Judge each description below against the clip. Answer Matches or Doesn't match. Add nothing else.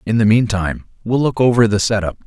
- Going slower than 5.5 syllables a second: Doesn't match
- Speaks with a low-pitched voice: Matches